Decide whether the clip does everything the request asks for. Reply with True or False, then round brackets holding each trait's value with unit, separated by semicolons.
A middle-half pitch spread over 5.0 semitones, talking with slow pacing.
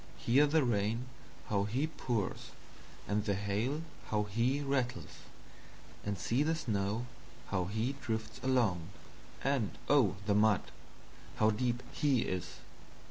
False (4.3 semitones; 130 wpm)